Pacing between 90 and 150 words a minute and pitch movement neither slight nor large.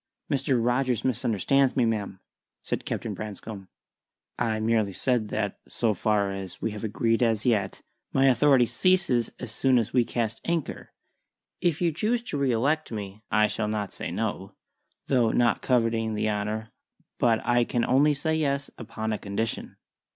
No: average, 165 wpm; average, 3.5 semitones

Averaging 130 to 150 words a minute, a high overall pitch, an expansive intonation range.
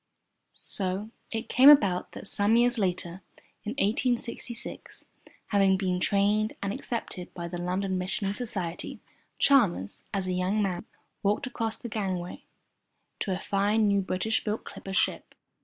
No: average, 140 wpm; high, 200 Hz; average, 3.2 semitones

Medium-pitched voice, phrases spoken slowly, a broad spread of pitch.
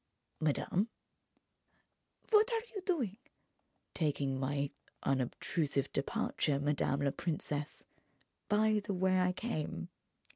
Yes: medium, 155 Hz; slow, 100 wpm; wide, 7.1 semitones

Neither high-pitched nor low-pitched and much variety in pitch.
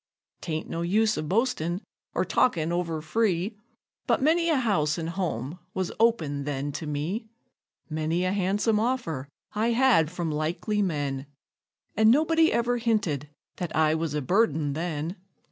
Yes: medium, 175 Hz; wide, 6.3 semitones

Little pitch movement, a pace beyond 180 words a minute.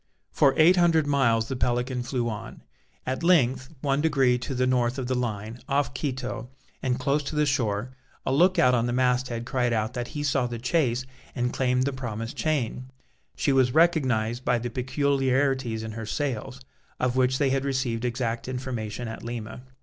Yes: narrow, 2.3 semitones; average, 190 wpm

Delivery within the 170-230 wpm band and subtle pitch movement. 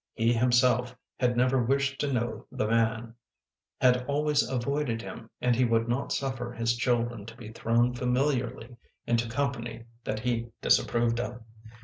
No: average, 150 wpm; narrow, 1.6 semitones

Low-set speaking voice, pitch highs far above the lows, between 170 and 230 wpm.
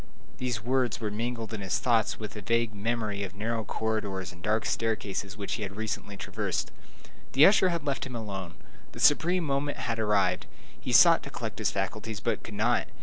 No: low, 110 Hz; average, 2.9 semitones; average, 195 wpm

